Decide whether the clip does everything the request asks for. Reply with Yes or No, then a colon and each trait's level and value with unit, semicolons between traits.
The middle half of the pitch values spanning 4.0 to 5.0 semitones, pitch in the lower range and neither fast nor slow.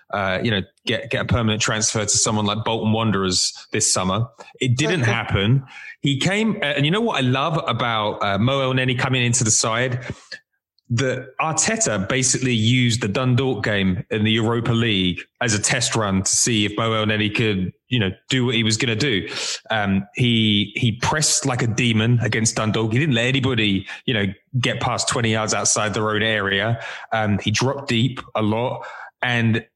No: average, 3.2 semitones; low, 115 Hz; average, 190 wpm